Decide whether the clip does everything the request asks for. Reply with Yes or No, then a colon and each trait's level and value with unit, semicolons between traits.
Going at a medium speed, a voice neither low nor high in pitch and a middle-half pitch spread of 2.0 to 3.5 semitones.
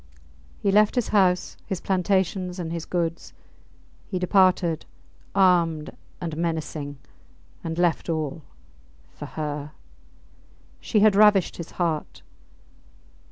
No: slow, 110 wpm; medium, 175 Hz; average, 2.8 semitones